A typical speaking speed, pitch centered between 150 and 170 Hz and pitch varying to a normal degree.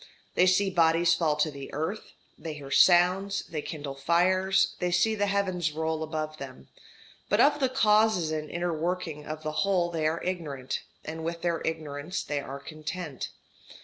Yes: average, 175 wpm; medium, 165 Hz; average, 3.0 semitones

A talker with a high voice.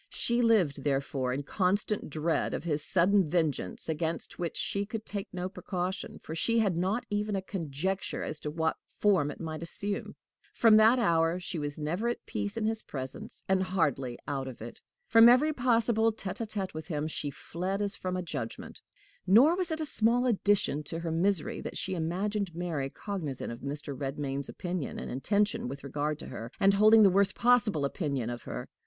No: medium, 180 Hz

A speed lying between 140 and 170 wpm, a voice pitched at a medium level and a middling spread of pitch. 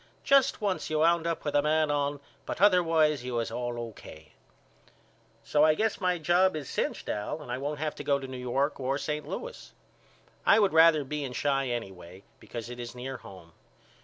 No: average, 200 wpm; medium, 145 Hz; average, 4.7 semitones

